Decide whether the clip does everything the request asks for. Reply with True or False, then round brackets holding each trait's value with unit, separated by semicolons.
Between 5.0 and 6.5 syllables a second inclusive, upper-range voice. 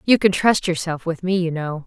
False (5.2 syllables/s; 175 Hz)